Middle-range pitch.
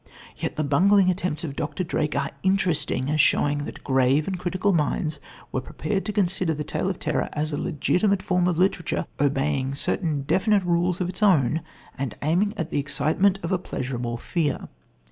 Yes: medium, 160 Hz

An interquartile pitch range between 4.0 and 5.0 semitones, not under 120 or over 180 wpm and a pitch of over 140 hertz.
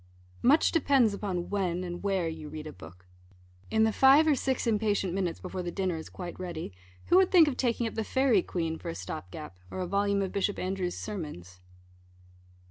No: average, 4.6 semitones; fast, 205 wpm; high, 190 Hz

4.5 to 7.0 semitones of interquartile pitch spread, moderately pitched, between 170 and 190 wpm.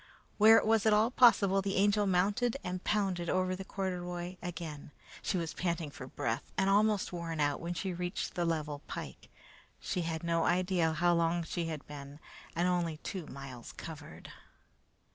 No: average, 3.0 semitones; medium, 175 Hz; average, 175 wpm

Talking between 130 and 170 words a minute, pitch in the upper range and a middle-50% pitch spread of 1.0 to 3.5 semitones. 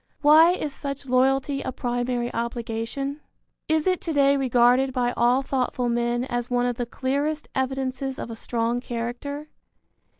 Yes: average, 155 wpm; very high, 255 Hz; narrow, 2.4 semitones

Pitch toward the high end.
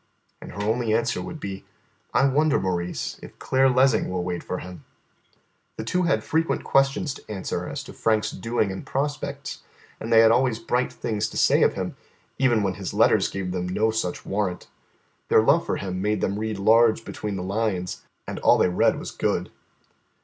No: low, 110 Hz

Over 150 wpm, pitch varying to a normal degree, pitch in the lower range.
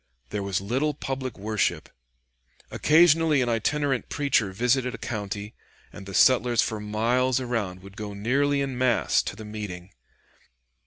No: average, 145 wpm; average, 4.4 semitones; low, 120 Hz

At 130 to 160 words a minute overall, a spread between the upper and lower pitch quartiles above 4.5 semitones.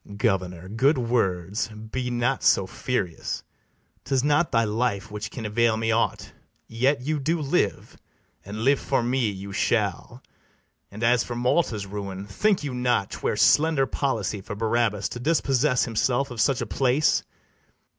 No: average, 155 wpm; average, 4.2 semitones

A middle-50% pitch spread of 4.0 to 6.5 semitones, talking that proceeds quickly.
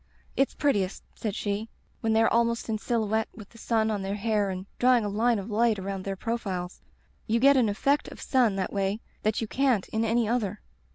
No: narrow, 2.6 semitones; fast, 215 wpm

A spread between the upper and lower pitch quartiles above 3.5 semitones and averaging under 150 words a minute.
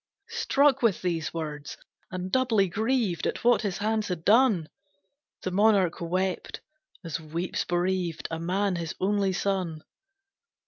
Yes: average, 3.9 semitones; slow, 135 wpm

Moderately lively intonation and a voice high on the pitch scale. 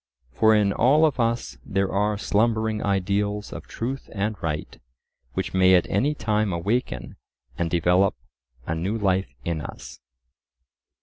No: average, 3.4 semitones; low, 100 Hz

